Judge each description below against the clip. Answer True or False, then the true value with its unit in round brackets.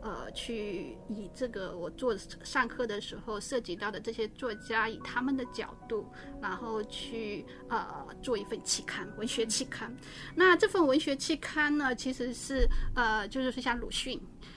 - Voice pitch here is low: False (240 Hz)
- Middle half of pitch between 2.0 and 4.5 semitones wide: True (3.3 semitones)